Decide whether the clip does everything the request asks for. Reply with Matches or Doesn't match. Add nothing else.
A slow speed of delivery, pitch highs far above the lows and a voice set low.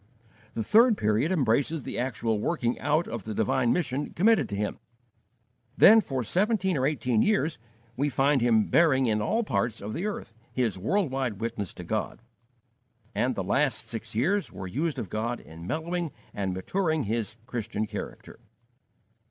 Doesn't match